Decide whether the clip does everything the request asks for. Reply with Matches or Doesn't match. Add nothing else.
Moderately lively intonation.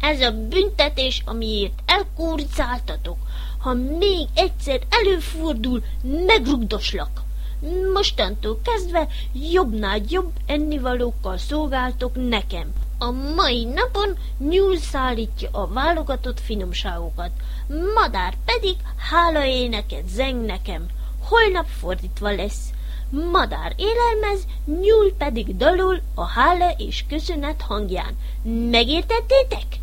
Doesn't match